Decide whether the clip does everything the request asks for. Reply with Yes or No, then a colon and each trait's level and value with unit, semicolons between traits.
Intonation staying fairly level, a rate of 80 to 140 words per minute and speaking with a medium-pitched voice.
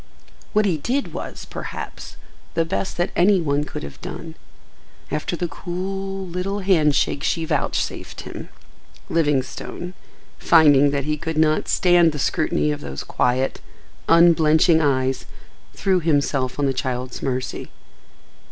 No: average, 3.8 semitones; slow, 135 wpm; medium, 160 Hz